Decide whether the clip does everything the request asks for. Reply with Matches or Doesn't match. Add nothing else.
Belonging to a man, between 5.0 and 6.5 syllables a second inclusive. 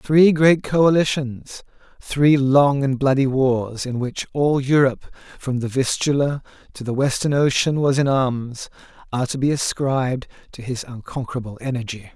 Doesn't match